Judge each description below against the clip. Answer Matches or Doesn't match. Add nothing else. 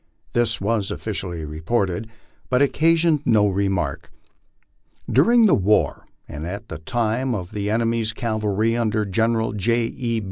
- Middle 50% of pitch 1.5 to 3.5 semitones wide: Matches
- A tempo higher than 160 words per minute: Doesn't match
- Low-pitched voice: Matches